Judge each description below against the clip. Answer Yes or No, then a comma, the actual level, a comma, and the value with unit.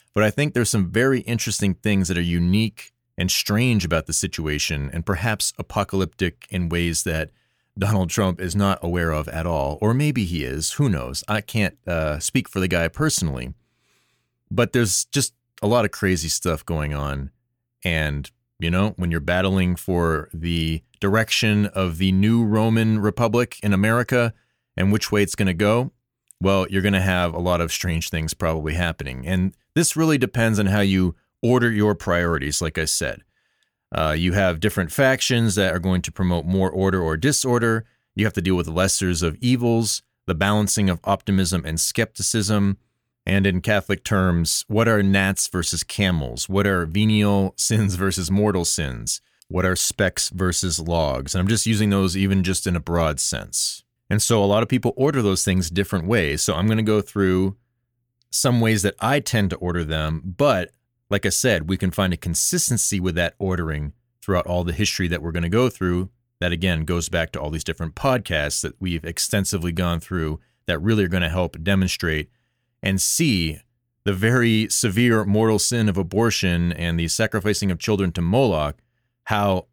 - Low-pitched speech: Yes, very low, 95 Hz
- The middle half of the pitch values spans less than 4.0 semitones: No, average, 4.3 semitones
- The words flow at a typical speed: Yes, average, 185 wpm